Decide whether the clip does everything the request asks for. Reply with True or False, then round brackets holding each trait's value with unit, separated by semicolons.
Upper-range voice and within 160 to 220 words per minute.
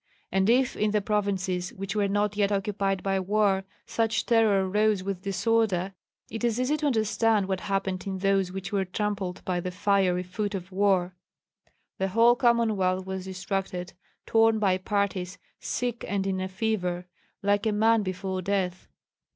True (195 Hz; 165 wpm)